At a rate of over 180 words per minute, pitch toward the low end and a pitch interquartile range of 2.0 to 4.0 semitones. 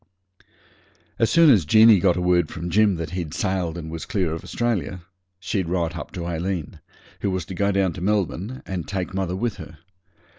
Yes: average, 195 wpm; very low, 90 Hz; average, 2.8 semitones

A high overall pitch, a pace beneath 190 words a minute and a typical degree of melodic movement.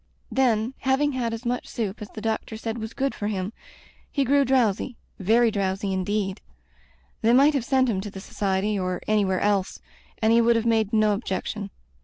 No: high, 220 Hz; average, 195 wpm; average, 3.1 semitones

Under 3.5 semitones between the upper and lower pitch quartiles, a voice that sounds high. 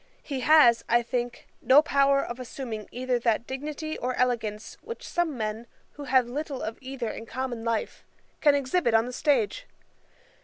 Yes: average, 3.1 semitones; very high, 255 Hz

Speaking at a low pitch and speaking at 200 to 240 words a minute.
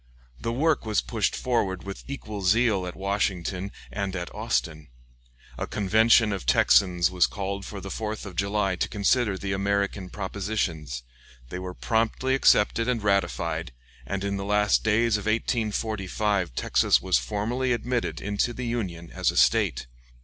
No: low, 100 Hz; average, 155 wpm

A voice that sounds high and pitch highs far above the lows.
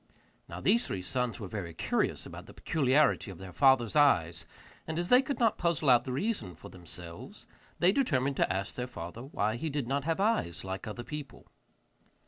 No: low, 125 Hz; wide, 8.6 semitones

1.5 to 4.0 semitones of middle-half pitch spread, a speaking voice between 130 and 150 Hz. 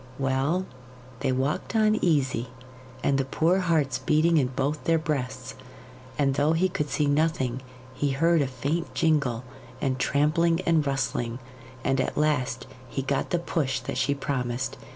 Yes: average, 3.6 semitones; medium, 140 Hz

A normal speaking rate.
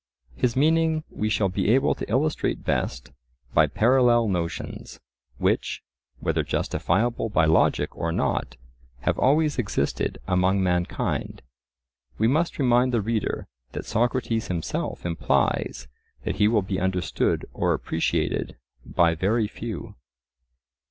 No: slow, 125 wpm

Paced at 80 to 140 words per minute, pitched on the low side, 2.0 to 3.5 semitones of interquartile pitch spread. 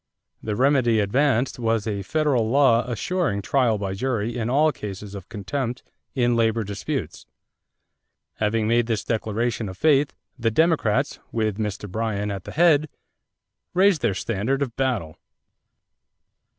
No: slow, 135 wpm; low, 115 Hz; average, 4.3 semitones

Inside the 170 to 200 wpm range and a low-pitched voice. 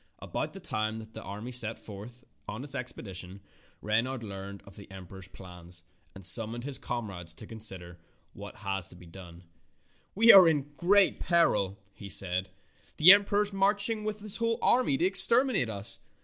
Yes: average, 175 wpm; low, 110 Hz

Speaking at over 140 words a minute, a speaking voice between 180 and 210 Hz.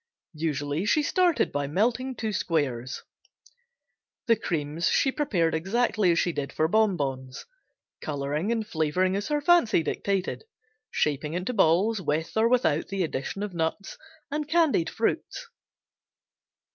No: slow, 135 wpm; medium, 185 Hz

